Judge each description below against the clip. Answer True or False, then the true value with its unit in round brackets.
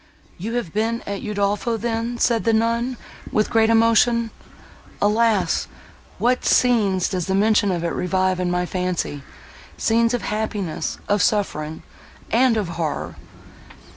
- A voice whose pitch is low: False (210 Hz)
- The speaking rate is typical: False (125 wpm)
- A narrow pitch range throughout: False (3.9 semitones)